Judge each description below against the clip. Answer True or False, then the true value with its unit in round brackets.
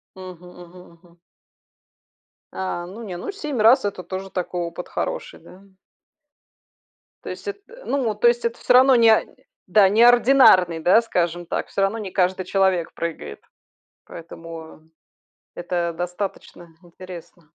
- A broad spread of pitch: False (4.3 semitones)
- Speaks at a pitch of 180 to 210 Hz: True (185 Hz)